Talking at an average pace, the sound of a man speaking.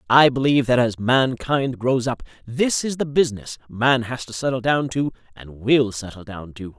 Yes: average, 195 wpm; male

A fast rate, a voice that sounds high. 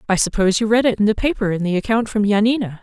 Yes: fast, 275 wpm; high, 210 Hz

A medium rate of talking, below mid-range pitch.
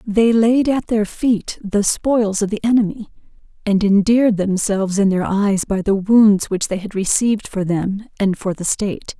No: average, 190 wpm; high, 205 Hz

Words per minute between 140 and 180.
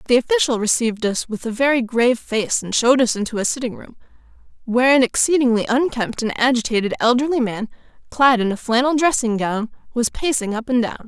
No: average, 190 wpm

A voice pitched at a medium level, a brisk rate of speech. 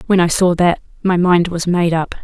Yes: medium, 175 Hz; fast, 240 wpm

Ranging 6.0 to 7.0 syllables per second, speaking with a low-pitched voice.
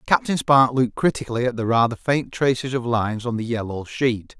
No: 5.7 syllables/s; low, 125 Hz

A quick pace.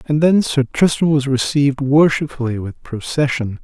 No: average, 150 wpm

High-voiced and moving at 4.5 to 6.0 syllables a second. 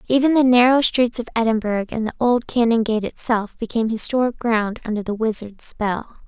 Yes: high, 230 Hz; 5.5 syllables/s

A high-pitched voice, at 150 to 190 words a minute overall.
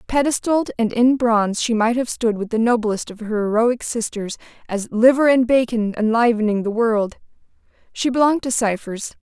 Yes: high, 230 Hz; average, 170 wpm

